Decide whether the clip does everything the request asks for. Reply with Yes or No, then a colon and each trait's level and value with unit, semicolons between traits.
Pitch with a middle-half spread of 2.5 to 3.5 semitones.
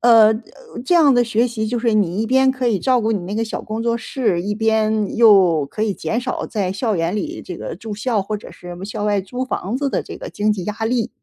Yes: average, 2.8 semitones